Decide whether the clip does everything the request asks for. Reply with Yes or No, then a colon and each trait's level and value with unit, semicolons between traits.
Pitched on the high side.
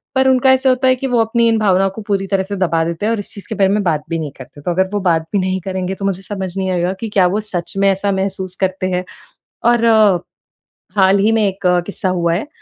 Yes: high, 195 Hz